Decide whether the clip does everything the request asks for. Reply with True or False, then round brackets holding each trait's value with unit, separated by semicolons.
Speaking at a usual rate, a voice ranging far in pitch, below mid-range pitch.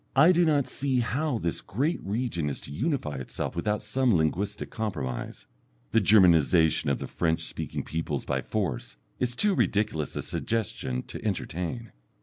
True (155 wpm; 7.7 semitones; 105 Hz)